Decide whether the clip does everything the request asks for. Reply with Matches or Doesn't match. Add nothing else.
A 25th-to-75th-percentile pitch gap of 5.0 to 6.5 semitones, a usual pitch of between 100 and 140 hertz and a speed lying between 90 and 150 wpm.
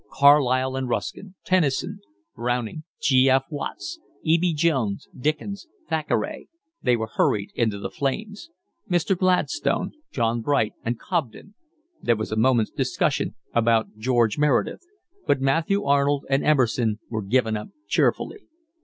Matches